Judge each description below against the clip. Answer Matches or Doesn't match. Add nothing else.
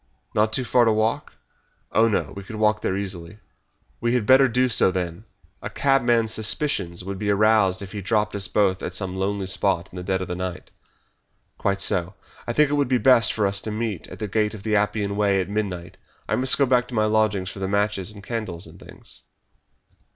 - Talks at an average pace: Doesn't match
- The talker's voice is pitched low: Matches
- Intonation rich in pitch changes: Doesn't match